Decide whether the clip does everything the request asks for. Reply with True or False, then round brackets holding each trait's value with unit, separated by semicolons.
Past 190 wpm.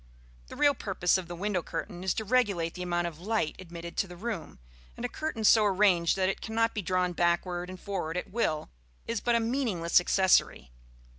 True (205 wpm)